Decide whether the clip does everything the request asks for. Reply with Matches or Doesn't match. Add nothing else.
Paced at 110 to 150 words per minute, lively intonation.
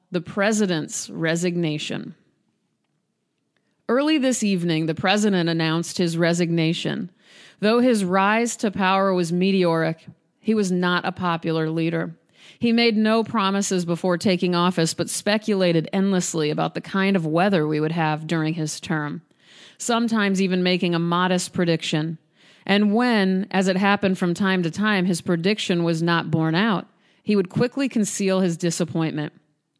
Doesn't match